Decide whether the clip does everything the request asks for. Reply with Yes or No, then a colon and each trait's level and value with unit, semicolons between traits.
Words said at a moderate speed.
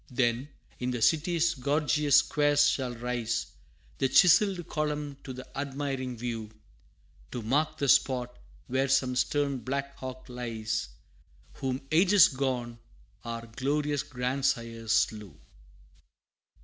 No: slow, 115 wpm